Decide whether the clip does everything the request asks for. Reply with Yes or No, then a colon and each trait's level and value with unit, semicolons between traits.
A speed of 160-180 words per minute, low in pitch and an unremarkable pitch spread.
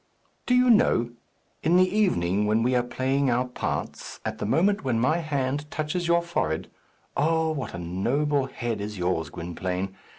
No: average, 170 wpm; low, 130 Hz; wide, 7.6 semitones